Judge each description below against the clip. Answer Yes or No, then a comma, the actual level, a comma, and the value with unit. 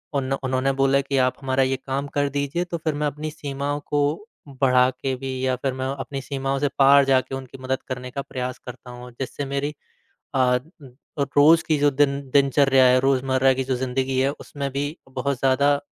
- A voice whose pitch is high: No, low, 135 Hz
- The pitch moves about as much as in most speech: No, narrow, 1.4 semitones